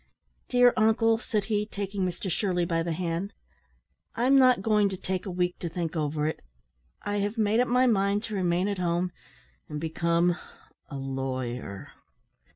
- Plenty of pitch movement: No, average, 4.0 semitones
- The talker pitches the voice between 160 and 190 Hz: Yes, medium, 185 Hz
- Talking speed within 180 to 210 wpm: No, average, 165 wpm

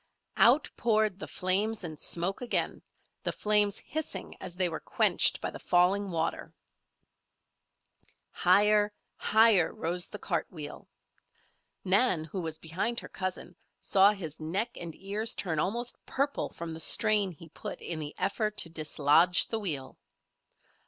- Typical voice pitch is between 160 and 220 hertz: Yes, high, 190 Hz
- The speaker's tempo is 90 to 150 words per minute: Yes, average, 145 wpm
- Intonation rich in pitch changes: No, average, 4.3 semitones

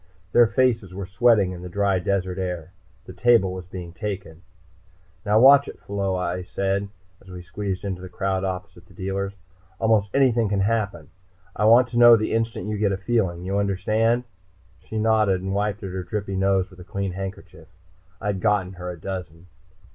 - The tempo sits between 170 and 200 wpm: Yes, average, 185 wpm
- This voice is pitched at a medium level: No, low, 100 Hz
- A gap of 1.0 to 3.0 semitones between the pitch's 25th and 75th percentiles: Yes, narrow, 2.5 semitones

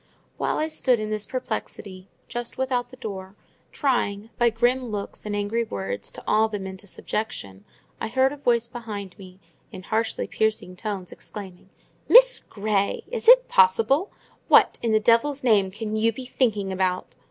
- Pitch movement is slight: No, average, 3.8 semitones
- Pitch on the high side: Yes, high, 220 Hz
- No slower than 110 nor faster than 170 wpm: Yes, average, 165 wpm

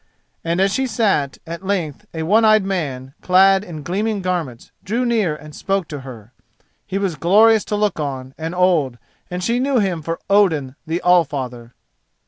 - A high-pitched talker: No, medium, 180 Hz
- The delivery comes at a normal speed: Yes, average, 175 wpm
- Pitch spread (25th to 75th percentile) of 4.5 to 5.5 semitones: Yes, average, 5.2 semitones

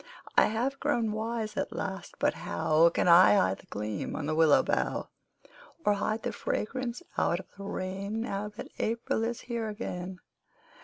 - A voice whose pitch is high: Yes, high, 210 Hz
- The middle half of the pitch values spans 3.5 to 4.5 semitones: Yes, average, 4.2 semitones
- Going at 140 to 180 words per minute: Yes, average, 170 wpm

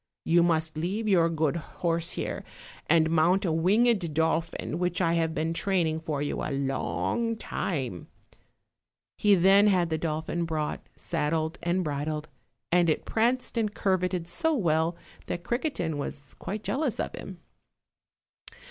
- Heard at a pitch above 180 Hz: No, medium, 170 Hz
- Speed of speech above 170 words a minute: No, average, 145 wpm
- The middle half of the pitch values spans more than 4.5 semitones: No, average, 3.3 semitones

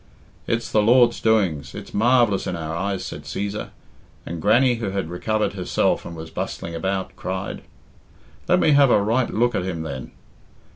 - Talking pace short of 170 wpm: No, average, 175 wpm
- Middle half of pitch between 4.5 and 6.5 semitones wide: Yes, average, 5.0 semitones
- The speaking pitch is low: Yes, low, 100 Hz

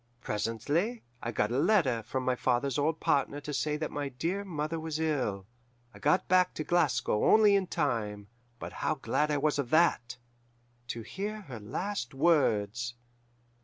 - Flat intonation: No, wide, 5.5 semitones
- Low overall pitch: No, medium, 145 Hz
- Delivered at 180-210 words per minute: No, average, 165 wpm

